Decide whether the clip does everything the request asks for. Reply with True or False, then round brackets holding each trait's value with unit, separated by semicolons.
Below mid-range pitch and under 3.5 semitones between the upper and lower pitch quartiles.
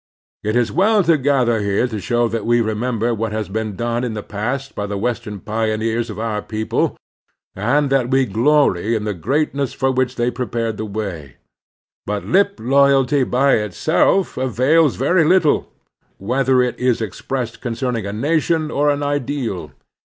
False (120 Hz; 4.1 semitones)